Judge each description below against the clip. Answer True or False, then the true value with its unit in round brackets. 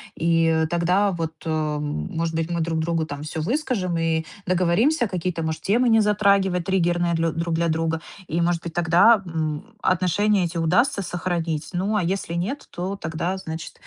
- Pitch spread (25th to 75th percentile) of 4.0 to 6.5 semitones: False (2.8 semitones)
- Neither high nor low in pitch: True (170 Hz)